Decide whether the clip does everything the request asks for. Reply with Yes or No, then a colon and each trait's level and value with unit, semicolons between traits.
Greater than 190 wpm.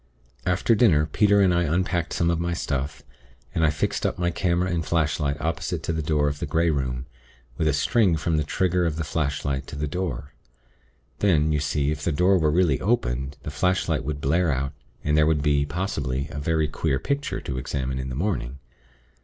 Yes: fast, 205 wpm